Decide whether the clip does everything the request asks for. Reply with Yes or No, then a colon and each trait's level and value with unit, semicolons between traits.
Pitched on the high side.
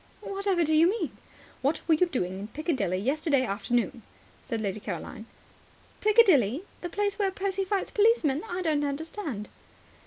Yes: very high, 310 Hz